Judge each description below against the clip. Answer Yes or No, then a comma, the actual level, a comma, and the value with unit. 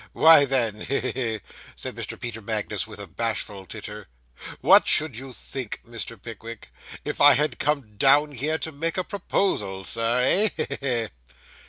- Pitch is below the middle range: Yes, low, 125 Hz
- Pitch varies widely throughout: No, average, 4.8 semitones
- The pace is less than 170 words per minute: No, average, 175 wpm